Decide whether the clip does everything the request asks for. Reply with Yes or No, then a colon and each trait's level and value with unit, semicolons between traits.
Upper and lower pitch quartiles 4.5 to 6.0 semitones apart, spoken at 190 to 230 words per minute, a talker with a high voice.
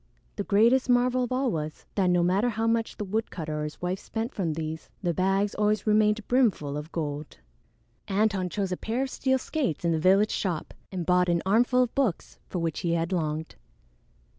Yes: average, 5.2 semitones; average, 200 wpm; high, 195 Hz